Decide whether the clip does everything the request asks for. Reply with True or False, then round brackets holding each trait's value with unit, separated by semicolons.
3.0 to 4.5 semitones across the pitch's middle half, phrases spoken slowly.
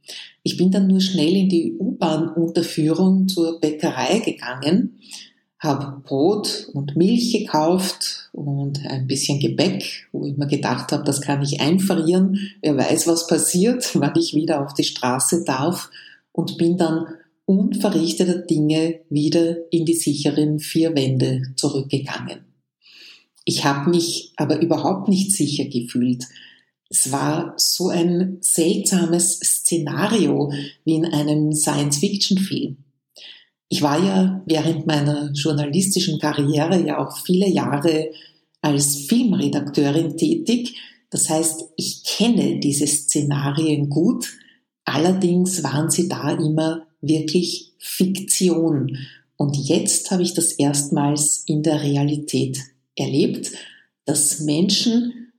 True (3.5 semitones; 120 wpm)